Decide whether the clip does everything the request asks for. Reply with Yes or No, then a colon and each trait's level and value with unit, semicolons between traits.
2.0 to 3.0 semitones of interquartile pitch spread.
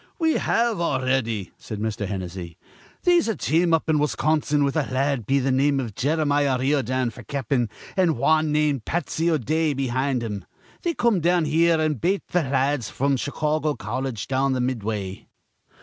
No: average, 4.1 semitones